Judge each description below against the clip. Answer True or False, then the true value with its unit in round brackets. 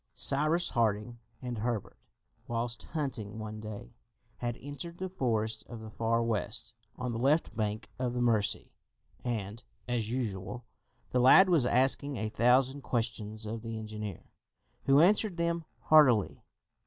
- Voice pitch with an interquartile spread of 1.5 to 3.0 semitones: False (3.6 semitones)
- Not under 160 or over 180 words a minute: False (140 wpm)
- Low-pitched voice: True (120 Hz)